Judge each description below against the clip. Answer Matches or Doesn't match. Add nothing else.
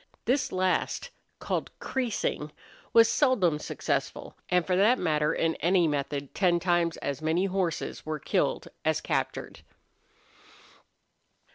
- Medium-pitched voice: Matches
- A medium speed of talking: Doesn't match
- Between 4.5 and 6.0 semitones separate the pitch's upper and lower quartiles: Doesn't match